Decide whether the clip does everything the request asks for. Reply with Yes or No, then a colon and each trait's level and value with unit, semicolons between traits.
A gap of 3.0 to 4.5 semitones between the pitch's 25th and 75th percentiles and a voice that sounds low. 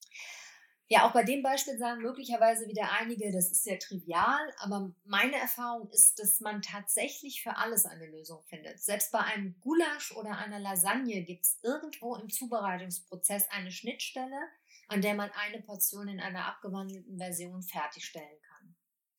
No: average, 4.0 semitones; high, 205 Hz